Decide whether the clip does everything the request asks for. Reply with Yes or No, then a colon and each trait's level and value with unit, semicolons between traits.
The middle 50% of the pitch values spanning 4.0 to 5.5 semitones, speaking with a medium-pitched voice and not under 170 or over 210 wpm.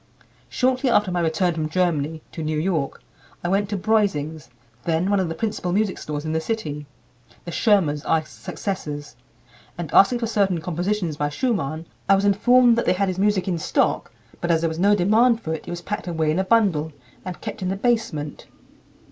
Yes: average, 4.5 semitones; medium, 180 Hz; fast, 205 wpm